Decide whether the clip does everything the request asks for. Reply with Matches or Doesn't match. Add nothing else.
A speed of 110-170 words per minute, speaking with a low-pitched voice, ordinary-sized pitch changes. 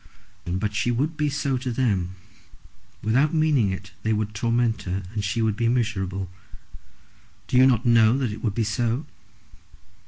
Matches